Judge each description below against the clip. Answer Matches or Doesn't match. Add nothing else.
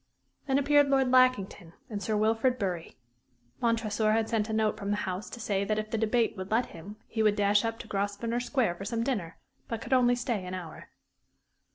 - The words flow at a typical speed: Doesn't match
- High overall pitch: Matches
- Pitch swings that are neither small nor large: Matches